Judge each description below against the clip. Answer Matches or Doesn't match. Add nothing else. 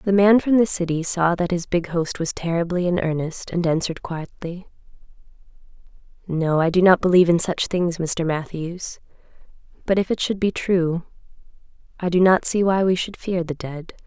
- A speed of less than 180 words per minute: Doesn't match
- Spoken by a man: Doesn't match